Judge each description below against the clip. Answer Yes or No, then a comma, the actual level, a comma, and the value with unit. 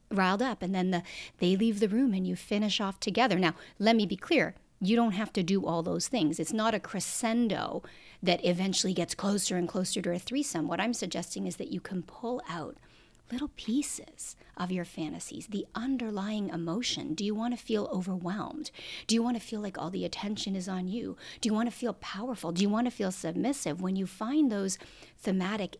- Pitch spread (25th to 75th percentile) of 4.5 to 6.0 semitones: No, average, 3.7 semitones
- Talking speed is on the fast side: Yes, fast, 215 wpm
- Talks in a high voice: Yes, high, 200 Hz